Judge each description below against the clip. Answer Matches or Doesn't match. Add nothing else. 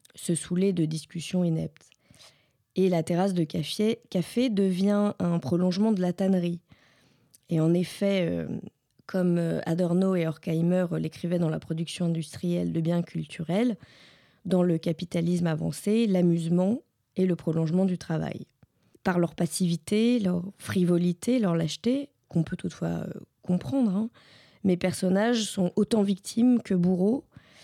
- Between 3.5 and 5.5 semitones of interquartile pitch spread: Doesn't match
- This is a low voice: Doesn't match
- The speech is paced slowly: Matches